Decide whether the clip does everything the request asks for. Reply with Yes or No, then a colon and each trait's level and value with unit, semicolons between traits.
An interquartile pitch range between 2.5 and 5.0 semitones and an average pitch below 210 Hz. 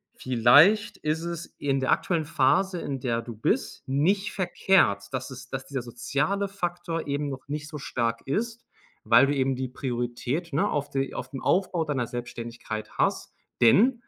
No: wide, 5.6 semitones; medium, 140 Hz